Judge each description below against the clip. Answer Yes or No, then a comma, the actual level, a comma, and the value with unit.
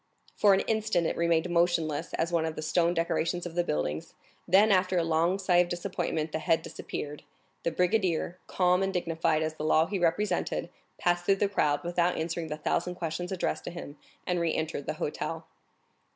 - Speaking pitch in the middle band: Yes, medium, 170 Hz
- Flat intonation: Yes, narrow, 2.0 semitones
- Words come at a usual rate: Yes, average, 195 wpm